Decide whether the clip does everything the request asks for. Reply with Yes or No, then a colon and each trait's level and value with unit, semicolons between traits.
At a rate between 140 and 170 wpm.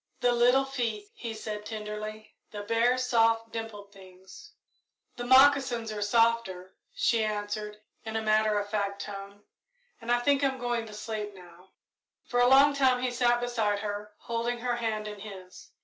Yes: average, 165 wpm